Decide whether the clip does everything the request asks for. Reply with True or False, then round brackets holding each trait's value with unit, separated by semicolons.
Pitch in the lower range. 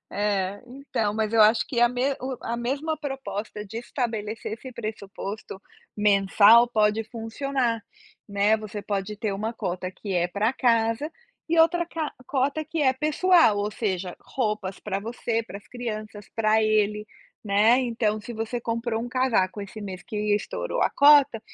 False (220 Hz)